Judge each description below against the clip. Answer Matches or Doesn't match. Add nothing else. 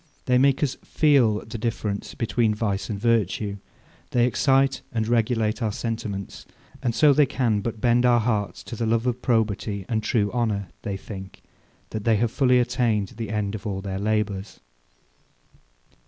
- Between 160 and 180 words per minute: Matches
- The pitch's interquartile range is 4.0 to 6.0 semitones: Doesn't match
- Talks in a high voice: Doesn't match